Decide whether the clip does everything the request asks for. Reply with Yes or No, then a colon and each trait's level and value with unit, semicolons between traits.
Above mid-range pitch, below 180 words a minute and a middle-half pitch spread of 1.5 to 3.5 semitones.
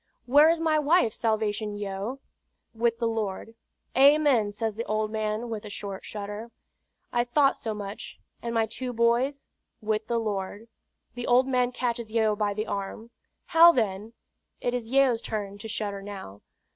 Yes: high, 225 Hz; average, 165 wpm; average, 2.7 semitones